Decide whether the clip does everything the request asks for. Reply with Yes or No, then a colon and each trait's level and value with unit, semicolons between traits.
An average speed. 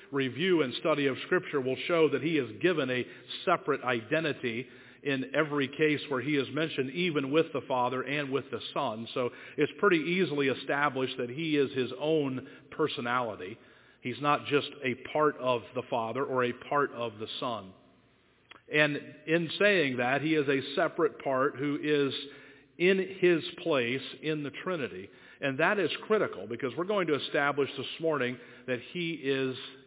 Yes: average, 170 wpm